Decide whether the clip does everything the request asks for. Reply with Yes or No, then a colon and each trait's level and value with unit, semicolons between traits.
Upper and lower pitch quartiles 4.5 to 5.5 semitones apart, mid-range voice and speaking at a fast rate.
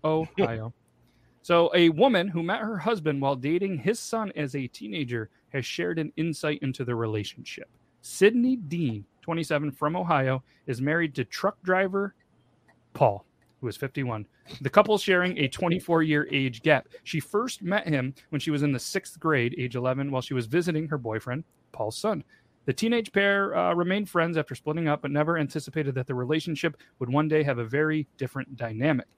No: average, 4.8 semitones; medium, 150 Hz; average, 180 wpm